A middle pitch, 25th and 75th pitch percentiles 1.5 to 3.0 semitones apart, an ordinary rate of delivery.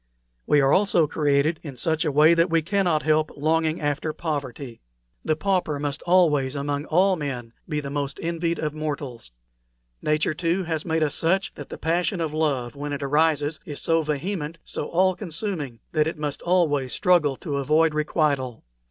Yes: medium, 155 Hz; narrow, 2.6 semitones; average, 180 wpm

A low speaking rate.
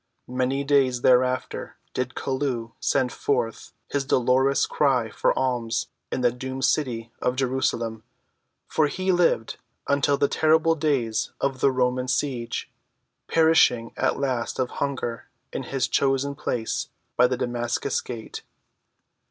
Yes: slow, 130 wpm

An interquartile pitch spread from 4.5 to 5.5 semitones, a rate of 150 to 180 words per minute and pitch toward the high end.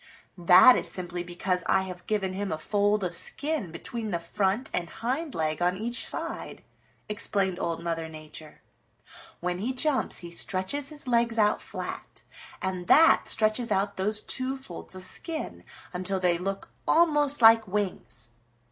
Yes: average, 4.9 semitones; average, 155 wpm; high, 195 Hz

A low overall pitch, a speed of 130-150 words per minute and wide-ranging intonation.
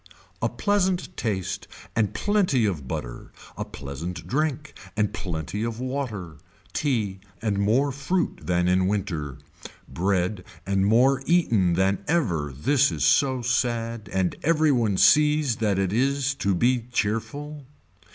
Yes: low, 110 Hz; slow, 135 wpm; wide, 6.7 semitones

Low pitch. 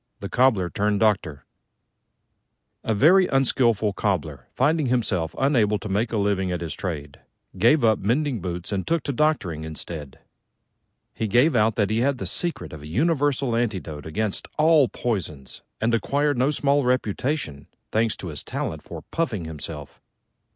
Yes: low, 110 Hz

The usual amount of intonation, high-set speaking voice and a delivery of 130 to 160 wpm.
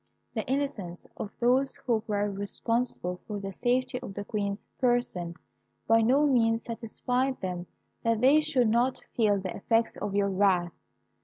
Yes: average, 3.8 semitones; high, 225 Hz; average, 155 wpm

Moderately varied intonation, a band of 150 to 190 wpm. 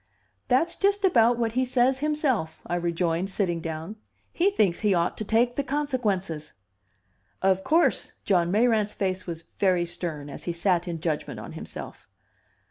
No: wide, 6.5 semitones; average, 160 wpm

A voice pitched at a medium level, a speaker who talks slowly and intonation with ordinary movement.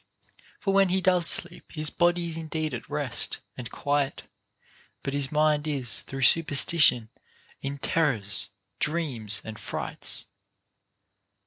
Yes: medium, 150 Hz; slow, 125 wpm; average, 3.8 semitones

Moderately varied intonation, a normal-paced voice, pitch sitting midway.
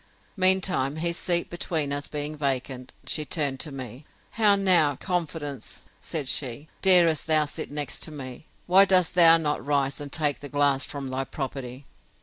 Yes: average, 3.7 semitones; average, 165 wpm; medium, 150 Hz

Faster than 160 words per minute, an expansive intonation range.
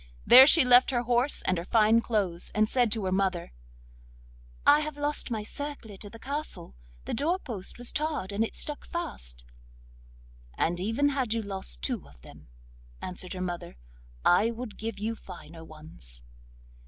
Yes: average, 170 wpm; wide, 5.8 semitones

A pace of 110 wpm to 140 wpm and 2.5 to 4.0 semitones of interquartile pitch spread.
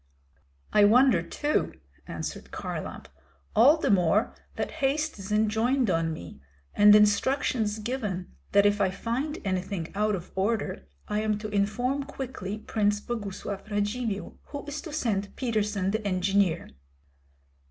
Yes: slow, 135 wpm; average, 3.7 semitones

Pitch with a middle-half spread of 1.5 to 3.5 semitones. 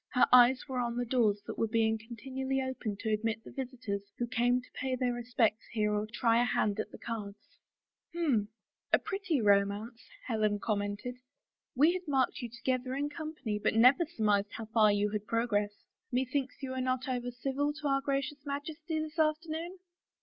No: average, 3.9 semitones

